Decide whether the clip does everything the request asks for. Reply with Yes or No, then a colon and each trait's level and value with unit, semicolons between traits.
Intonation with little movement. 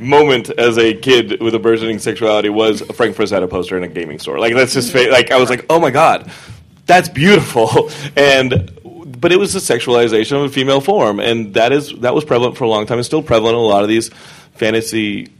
No: average, 4.2 semitones